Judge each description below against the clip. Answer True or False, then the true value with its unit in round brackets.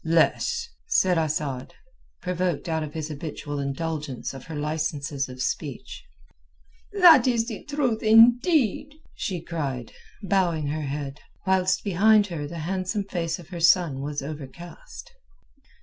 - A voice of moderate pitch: True (165 Hz)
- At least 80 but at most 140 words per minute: True (135 wpm)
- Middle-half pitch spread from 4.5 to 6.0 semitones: True (5.5 semitones)